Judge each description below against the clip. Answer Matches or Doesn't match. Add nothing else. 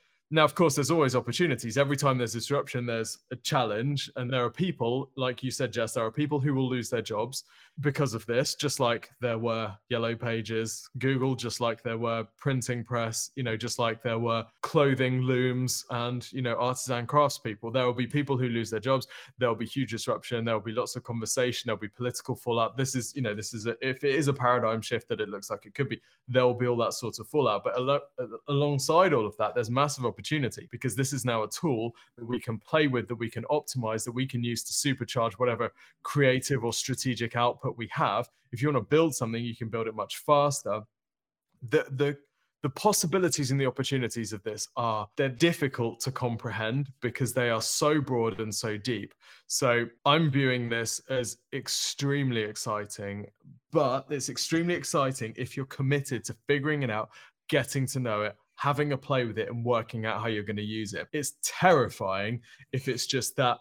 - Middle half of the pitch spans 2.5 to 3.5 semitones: Matches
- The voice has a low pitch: Matches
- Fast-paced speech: Matches